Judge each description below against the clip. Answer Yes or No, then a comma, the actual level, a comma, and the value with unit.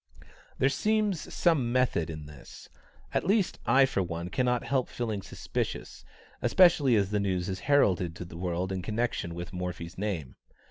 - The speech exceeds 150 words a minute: Yes, average, 165 wpm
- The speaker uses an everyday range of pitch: No, wide, 6.8 semitones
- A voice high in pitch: No, low, 100 Hz